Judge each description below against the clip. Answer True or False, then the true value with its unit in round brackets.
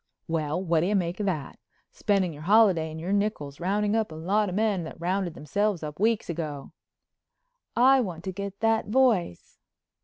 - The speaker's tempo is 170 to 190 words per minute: True (185 wpm)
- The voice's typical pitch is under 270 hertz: True (190 Hz)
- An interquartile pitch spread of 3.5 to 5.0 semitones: True (4.5 semitones)